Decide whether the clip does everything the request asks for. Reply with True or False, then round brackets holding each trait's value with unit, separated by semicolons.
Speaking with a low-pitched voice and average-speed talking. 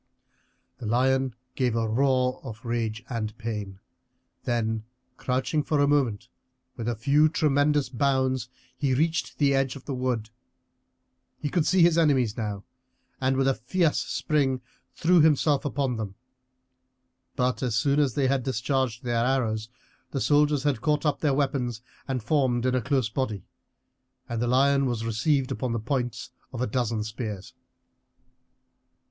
True (130 Hz; 155 wpm)